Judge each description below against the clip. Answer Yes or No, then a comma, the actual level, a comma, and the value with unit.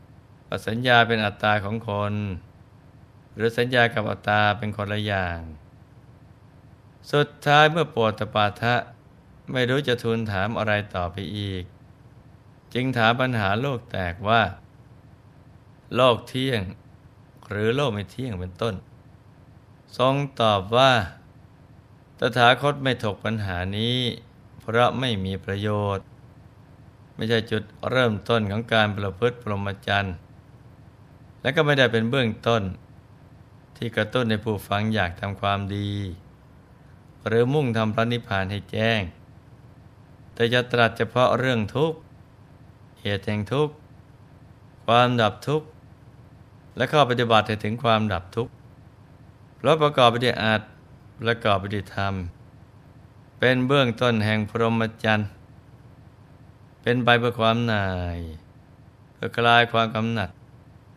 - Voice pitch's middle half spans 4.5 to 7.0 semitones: No, average, 3.5 semitones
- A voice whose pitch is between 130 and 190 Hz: No, low, 115 Hz